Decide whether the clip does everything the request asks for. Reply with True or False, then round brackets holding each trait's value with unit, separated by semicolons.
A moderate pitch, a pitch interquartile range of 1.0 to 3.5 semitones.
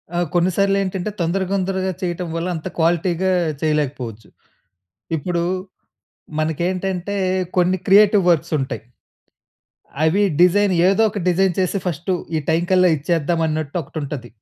True (175 Hz; 2.9 semitones)